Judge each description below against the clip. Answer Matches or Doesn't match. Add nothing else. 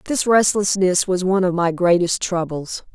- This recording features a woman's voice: Matches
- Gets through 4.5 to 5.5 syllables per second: Matches